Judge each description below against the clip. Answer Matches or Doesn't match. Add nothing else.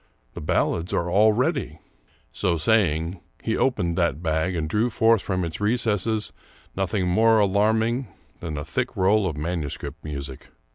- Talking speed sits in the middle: Matches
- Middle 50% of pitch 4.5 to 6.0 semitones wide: Matches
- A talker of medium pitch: Doesn't match